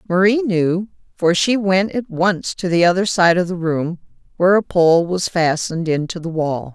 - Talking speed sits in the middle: Yes, average, 195 wpm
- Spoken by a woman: Yes, female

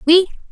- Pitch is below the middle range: No, very high, 350 Hz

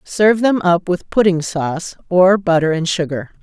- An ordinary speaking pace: Yes, average, 175 wpm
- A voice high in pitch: No, medium, 180 Hz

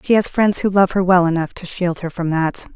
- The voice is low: No, medium, 180 Hz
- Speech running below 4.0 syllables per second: No, 5.4 syllables/s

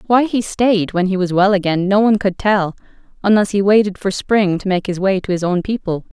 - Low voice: No, high, 195 Hz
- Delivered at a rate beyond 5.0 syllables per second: Yes, 5.5 syllables/s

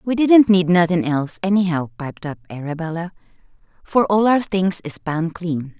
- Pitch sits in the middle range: Yes, medium, 180 Hz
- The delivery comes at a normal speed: Yes, average, 165 wpm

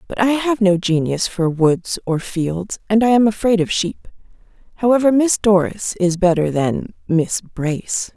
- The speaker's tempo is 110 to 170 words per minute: Yes, average, 160 wpm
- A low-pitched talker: No, high, 195 Hz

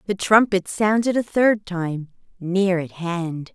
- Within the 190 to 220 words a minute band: No, average, 150 wpm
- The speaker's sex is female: Yes, female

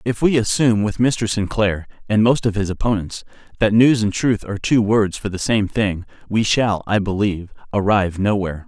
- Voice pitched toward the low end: Yes, low, 105 Hz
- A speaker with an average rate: Yes, average, 195 wpm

